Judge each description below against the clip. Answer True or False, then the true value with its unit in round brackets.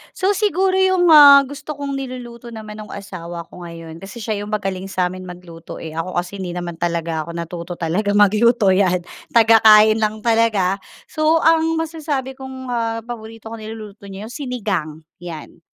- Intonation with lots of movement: True (6.3 semitones)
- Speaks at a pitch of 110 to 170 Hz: False (215 Hz)